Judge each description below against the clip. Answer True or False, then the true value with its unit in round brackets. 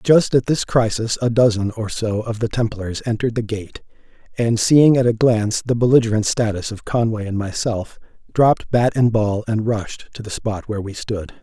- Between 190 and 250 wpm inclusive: True (200 wpm)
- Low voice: True (110 Hz)